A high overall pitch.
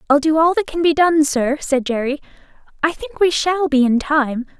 Yes: very high, 295 Hz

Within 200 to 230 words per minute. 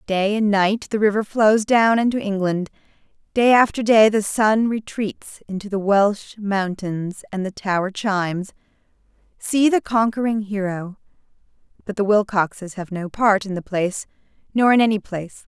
No: average, 155 wpm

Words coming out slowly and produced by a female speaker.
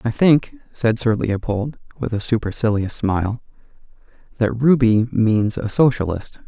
No: slow, 130 wpm; male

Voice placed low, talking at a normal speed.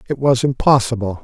Yes: low, 125 Hz; average, 145 wpm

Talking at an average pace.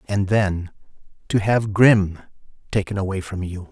No: slow, 130 wpm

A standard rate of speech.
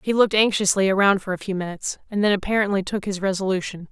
No: fast, 215 wpm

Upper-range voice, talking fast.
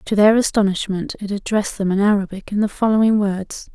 No: high, 205 Hz; average, 190 wpm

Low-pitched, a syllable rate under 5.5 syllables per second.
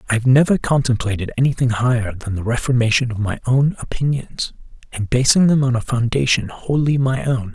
No: low, 125 Hz; 5.6 syllables/s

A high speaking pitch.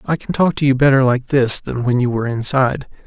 No: low, 130 Hz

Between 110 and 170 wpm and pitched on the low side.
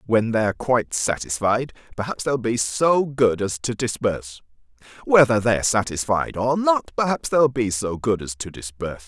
Yes: average, 165 wpm; low, 115 Hz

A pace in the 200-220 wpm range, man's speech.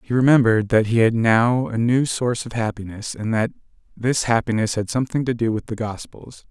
Yes: fast, 205 wpm; male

